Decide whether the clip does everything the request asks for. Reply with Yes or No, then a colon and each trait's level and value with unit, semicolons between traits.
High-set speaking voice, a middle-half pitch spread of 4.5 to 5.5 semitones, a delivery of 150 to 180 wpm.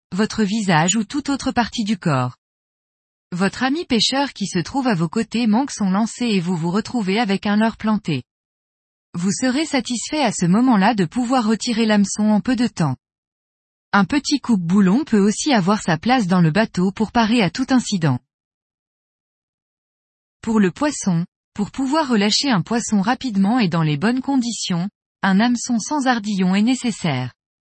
Yes: high, 215 Hz; average, 5.1 semitones; average, 170 wpm